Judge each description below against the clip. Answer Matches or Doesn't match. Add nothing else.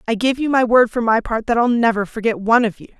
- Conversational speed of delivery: Doesn't match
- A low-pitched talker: Doesn't match